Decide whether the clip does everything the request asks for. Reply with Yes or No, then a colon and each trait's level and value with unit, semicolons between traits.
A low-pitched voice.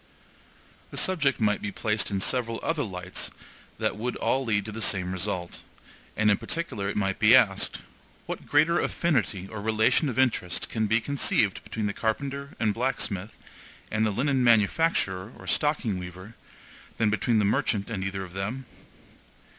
Yes: low, 110 Hz